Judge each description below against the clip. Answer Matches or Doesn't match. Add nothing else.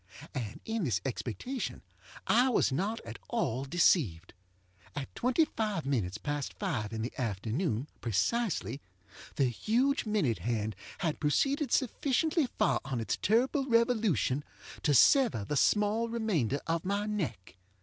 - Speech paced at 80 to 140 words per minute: Matches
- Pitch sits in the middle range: Matches